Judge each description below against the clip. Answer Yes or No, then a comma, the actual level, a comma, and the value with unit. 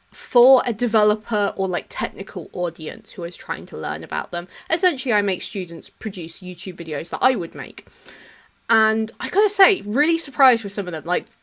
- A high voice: Yes, high, 210 Hz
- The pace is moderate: Yes, average, 190 wpm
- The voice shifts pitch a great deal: Yes, wide, 5.9 semitones